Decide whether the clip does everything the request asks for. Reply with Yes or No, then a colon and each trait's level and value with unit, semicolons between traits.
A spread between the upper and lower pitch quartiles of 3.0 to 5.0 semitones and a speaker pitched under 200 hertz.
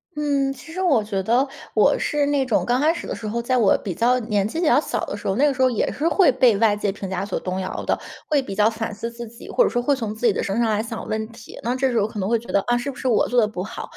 No: average, 4.1 semitones; high, 235 Hz